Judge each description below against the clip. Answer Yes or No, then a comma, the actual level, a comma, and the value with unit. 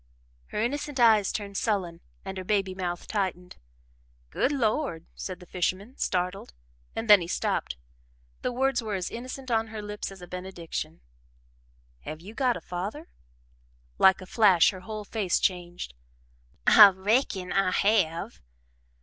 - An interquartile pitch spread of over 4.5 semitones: No, average, 3.6 semitones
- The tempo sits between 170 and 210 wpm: No, average, 150 wpm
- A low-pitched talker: No, high, 195 Hz